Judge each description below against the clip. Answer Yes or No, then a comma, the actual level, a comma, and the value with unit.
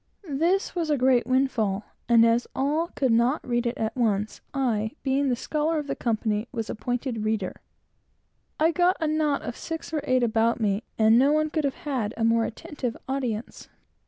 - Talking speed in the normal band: Yes, average, 190 wpm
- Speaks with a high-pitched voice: Yes, very high, 250 Hz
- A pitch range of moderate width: Yes, average, 4.6 semitones